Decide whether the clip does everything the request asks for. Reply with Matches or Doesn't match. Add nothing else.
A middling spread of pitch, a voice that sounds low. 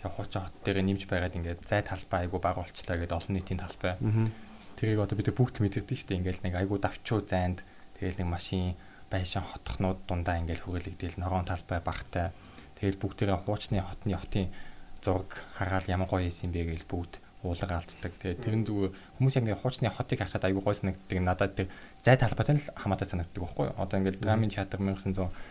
Doesn't match